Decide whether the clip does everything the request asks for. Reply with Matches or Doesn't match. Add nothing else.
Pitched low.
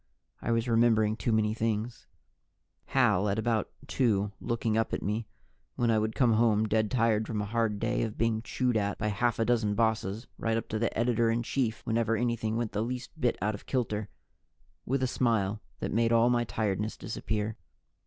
Matches